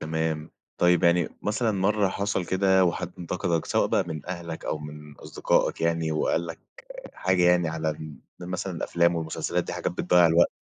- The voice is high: No, very low, 85 Hz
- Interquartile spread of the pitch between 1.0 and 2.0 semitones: No, narrow, 2.4 semitones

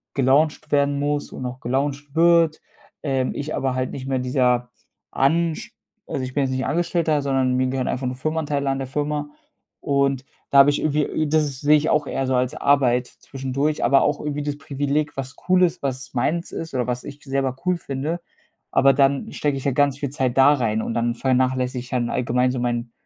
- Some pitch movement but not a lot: No, narrow, 2.3 semitones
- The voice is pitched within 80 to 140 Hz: Yes, low, 135 Hz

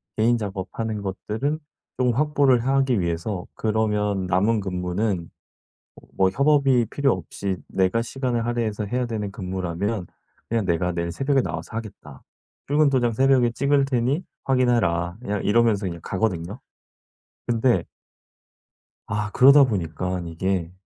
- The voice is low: Yes, low, 110 Hz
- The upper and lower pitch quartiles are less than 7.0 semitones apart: Yes, average, 5.1 semitones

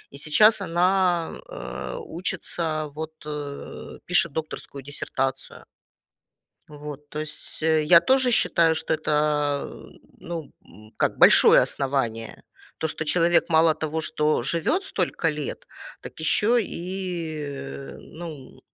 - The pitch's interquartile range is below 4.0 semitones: Yes, average, 2.8 semitones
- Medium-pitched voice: Yes, medium, 155 Hz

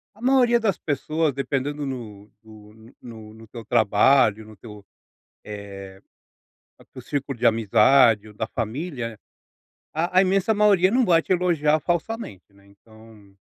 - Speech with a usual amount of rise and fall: No, wide, 7.4 semitones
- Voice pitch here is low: Yes, low, 120 Hz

